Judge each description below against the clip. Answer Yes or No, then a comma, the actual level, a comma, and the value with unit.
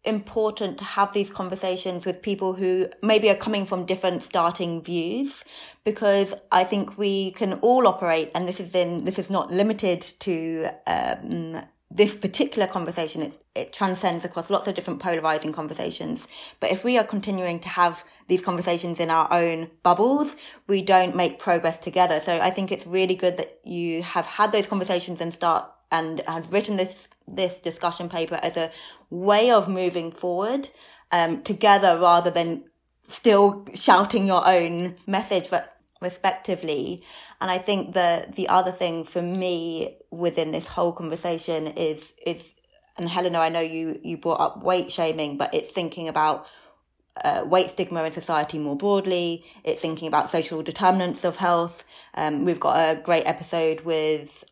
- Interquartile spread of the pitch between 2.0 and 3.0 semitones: Yes, average, 2.7 semitones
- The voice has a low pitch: No, medium, 180 Hz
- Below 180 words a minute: Yes, average, 165 wpm